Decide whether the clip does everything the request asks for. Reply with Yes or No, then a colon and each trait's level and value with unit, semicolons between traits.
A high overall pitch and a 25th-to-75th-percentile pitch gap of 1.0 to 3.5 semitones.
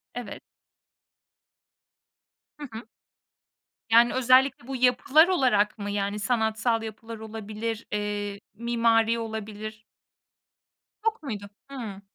Yes: high, 225 Hz; narrow, 2.6 semitones